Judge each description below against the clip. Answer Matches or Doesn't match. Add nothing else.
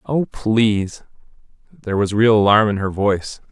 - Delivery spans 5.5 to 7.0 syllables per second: Doesn't match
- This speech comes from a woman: Doesn't match